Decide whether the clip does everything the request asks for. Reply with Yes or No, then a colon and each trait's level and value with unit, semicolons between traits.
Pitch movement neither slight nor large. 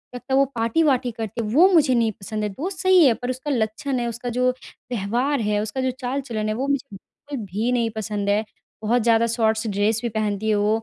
Yes: average, 3.3 semitones